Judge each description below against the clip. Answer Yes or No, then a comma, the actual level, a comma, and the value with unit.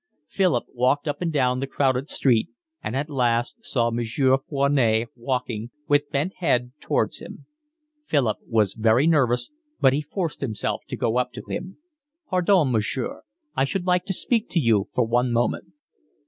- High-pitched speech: No, low, 130 Hz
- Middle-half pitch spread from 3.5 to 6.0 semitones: Yes, average, 4.0 semitones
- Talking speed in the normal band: Yes, average, 165 wpm